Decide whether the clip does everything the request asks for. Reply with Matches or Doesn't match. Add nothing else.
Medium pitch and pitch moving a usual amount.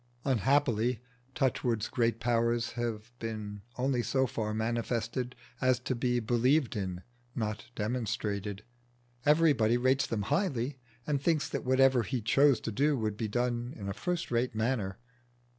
Doesn't match